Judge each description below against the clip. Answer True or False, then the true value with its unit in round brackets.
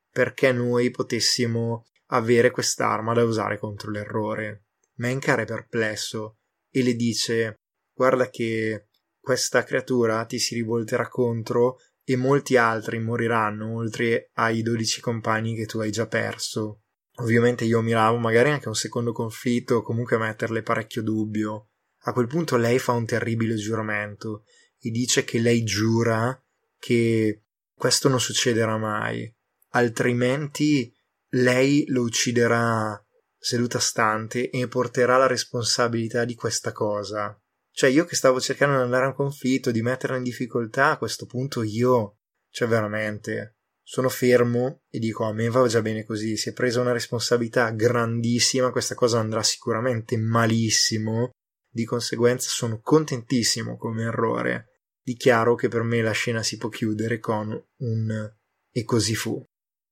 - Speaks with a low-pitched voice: True (115 Hz)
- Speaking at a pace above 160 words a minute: False (145 wpm)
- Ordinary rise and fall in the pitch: False (2.0 semitones)